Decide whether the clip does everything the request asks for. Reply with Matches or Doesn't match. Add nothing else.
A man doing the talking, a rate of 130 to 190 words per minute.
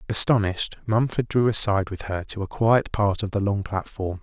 Doesn't match